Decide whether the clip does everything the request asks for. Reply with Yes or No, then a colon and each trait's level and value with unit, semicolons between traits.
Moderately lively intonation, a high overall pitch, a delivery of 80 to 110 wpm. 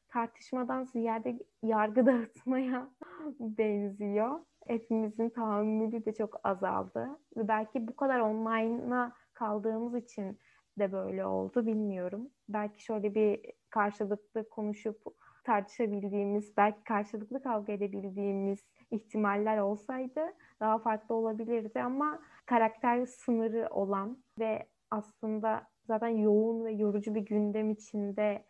No: narrow, 2.2 semitones; high, 220 Hz; average, 105 wpm